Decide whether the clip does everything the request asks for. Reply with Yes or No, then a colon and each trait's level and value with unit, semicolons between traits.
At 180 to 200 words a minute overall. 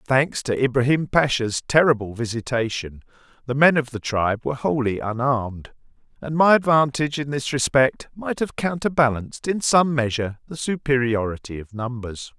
No: average, 145 wpm